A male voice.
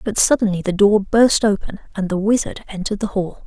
No: female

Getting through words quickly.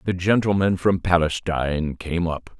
No: average, 140 wpm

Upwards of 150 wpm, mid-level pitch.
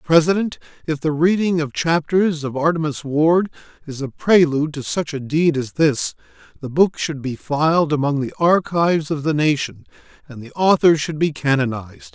Yes: average, 175 wpm; medium, 155 Hz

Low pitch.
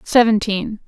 No: high, 215 Hz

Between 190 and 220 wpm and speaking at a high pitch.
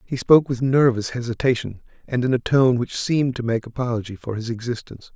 No: average, 200 wpm; low, 120 Hz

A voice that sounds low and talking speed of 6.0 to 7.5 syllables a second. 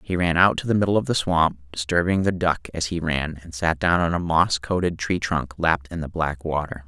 No: very low, 85 Hz; 5.4 syllables/s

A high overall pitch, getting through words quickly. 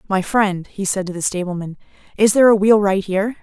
Yes: high, 200 Hz; fast, 210 wpm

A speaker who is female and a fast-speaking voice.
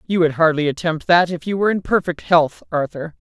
Yes: female; fast, 215 wpm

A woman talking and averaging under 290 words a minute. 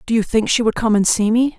No: female; fast, 340 wpm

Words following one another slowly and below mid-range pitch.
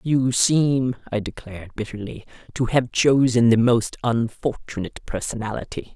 Yes: slow, 120 wpm; low, 120 Hz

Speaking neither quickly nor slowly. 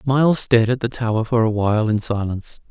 No: fast, 220 wpm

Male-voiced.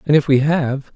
Yes: male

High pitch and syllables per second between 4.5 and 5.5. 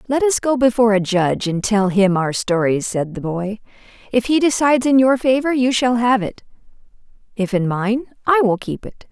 Yes: high, 225 Hz; 5.2 syllables/s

